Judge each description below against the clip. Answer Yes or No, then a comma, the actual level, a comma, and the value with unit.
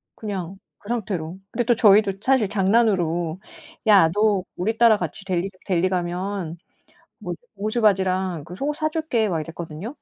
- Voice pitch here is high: Yes, high, 195 Hz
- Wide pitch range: No, average, 3.8 semitones